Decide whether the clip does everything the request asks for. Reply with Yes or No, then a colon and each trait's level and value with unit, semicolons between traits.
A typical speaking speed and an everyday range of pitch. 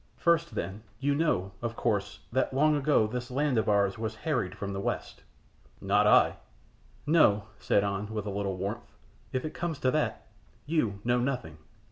No: average, 175 wpm; wide, 6.1 semitones